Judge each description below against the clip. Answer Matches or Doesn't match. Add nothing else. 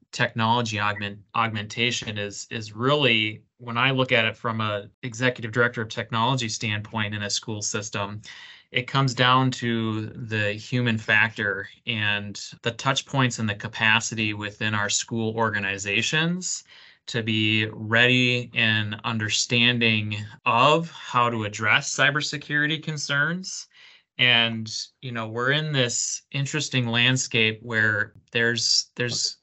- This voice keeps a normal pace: Doesn't match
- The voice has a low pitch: Matches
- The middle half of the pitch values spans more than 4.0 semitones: Doesn't match